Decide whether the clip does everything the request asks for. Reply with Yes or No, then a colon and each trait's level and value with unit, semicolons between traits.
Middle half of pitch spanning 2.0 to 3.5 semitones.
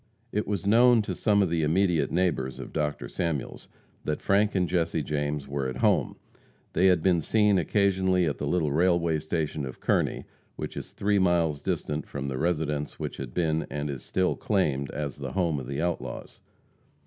No: average, 4.1 semitones